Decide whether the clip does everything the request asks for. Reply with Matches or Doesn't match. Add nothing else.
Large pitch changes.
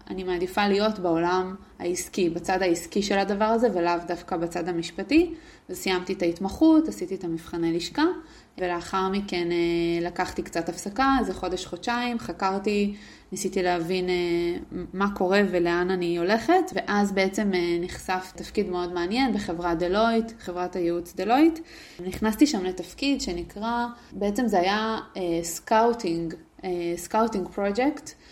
Doesn't match